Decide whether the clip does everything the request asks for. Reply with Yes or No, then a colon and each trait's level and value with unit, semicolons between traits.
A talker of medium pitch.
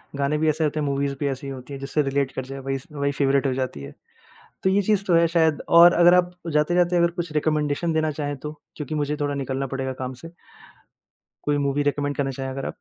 Yes: medium, 145 Hz